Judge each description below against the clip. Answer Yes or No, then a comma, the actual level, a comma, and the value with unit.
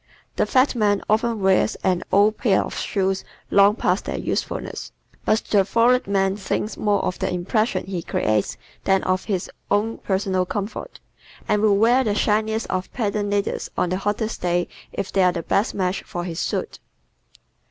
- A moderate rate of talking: Yes, average, 175 wpm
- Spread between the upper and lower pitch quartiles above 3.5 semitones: No, narrow, 2.4 semitones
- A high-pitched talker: Yes, high, 200 Hz